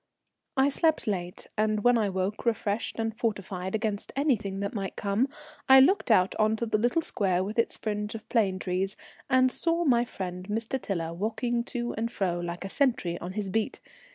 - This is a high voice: Yes, high, 215 Hz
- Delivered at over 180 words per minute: Yes, average, 190 wpm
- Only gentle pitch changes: No, average, 3.8 semitones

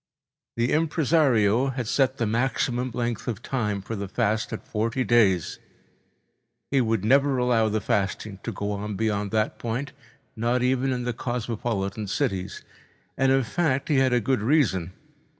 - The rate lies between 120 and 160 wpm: Yes, average, 150 wpm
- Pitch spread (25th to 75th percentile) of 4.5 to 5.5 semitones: No, average, 3.8 semitones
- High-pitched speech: No, low, 115 Hz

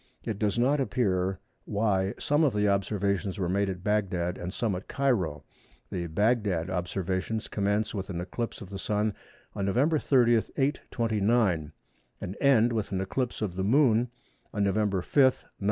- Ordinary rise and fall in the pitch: Yes, average, 3.7 semitones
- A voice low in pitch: Yes, low, 105 Hz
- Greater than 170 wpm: No, average, 165 wpm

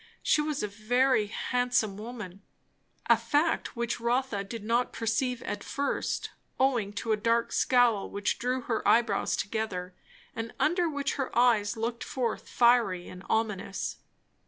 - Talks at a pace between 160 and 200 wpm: No, average, 145 wpm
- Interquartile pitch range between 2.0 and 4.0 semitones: Yes, average, 3.2 semitones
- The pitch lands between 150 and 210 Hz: No, high, 230 Hz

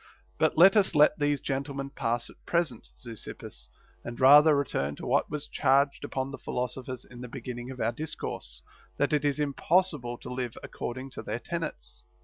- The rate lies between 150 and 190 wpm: Yes, average, 175 wpm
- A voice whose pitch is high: No, low, 135 Hz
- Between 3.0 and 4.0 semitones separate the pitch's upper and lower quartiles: Yes, average, 3.4 semitones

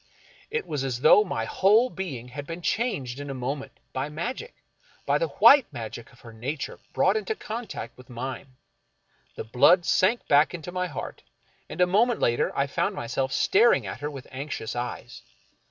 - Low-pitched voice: No, medium, 145 Hz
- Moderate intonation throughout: No, wide, 7.7 semitones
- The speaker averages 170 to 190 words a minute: Yes, average, 185 wpm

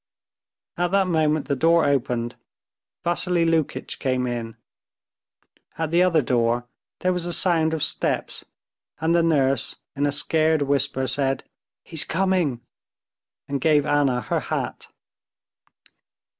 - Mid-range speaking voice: Yes, medium, 150 Hz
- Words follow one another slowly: Yes, slow, 130 wpm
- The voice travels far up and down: No, average, 3.9 semitones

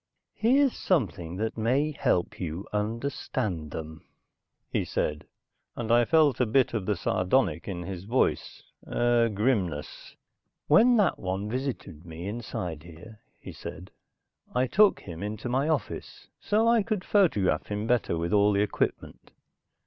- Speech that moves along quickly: No, average, 145 wpm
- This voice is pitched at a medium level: No, low, 110 Hz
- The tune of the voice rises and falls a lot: Yes, wide, 7.0 semitones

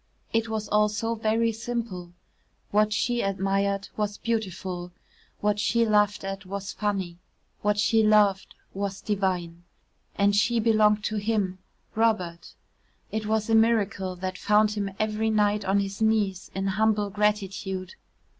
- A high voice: Yes, high, 210 Hz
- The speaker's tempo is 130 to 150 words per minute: Yes, average, 140 wpm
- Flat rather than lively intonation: Yes, narrow, 2.0 semitones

